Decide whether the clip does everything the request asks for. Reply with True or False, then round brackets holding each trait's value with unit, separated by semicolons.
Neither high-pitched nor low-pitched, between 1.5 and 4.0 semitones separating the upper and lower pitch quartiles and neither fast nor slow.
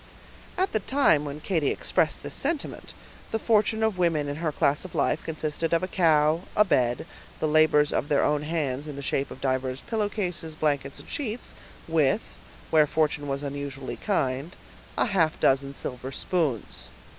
False (155 Hz; 4.4 semitones; 170 wpm)